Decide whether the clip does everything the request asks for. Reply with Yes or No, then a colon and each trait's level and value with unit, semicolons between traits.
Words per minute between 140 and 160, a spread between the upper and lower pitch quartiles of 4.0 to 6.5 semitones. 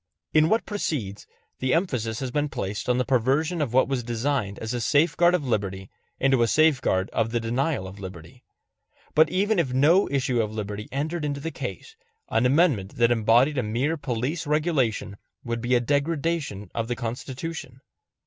No: average, 175 wpm; average, 5.1 semitones